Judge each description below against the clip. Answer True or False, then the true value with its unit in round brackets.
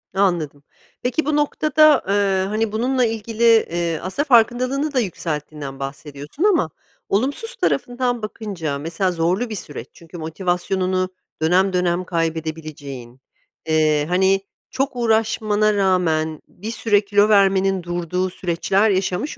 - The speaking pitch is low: False (190 Hz)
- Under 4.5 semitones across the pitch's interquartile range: False (5.4 semitones)